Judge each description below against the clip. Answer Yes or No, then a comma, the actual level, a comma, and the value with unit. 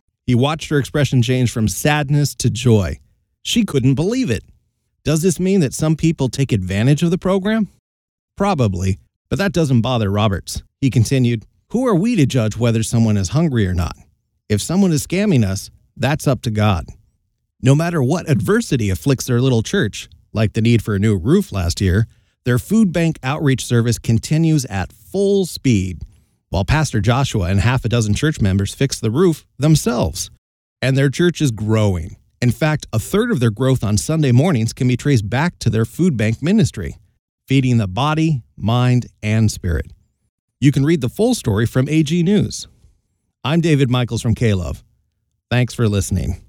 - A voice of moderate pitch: No, low, 120 Hz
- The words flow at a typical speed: Yes, average, 180 wpm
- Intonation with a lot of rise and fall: Yes, wide, 6.2 semitones